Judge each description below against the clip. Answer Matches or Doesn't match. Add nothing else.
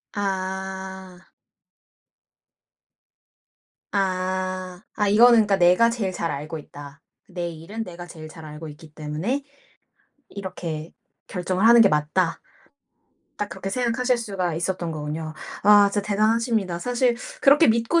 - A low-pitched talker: Doesn't match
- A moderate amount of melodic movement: Matches